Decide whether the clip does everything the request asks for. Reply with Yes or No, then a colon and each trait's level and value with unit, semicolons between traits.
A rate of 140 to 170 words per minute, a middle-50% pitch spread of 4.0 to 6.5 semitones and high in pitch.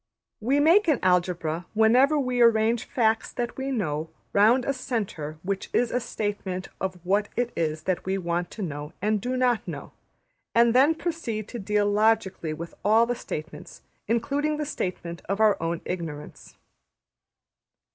Yes: average, 160 wpm; wide, 5.4 semitones; high, 215 Hz